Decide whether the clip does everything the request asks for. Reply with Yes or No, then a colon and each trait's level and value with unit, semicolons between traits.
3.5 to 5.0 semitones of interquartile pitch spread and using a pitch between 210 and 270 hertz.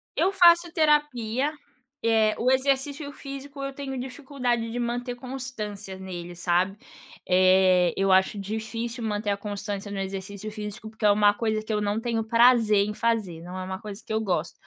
Yes: average, 4.2 semitones; high, 220 Hz